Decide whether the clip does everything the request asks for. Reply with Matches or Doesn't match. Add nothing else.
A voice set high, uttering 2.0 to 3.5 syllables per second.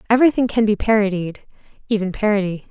Doesn't match